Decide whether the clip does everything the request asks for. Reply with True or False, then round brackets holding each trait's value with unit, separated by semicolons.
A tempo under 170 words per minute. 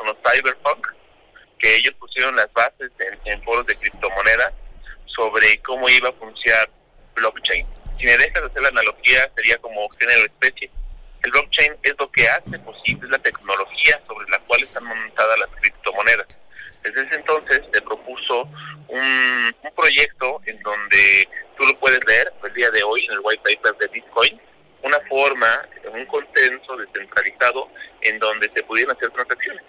True (160 wpm)